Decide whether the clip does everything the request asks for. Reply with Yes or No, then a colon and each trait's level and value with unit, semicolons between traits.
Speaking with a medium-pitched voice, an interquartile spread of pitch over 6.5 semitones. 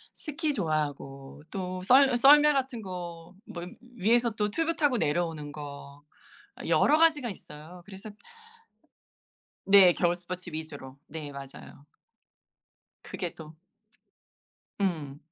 Yes: medium, 180 Hz; wide, 7.6 semitones